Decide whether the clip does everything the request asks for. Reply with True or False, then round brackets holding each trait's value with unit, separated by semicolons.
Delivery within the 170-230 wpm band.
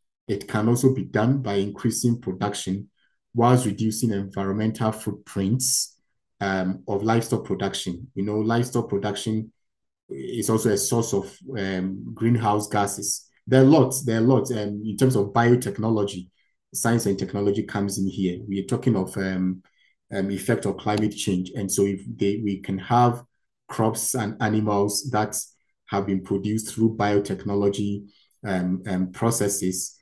False (150 wpm)